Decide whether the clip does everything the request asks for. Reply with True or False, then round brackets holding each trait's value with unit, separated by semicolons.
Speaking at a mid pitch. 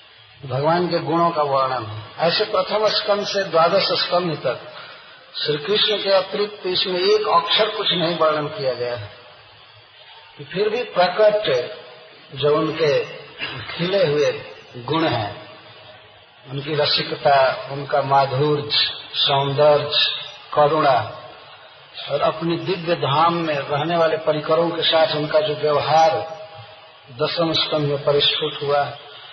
True (155 Hz)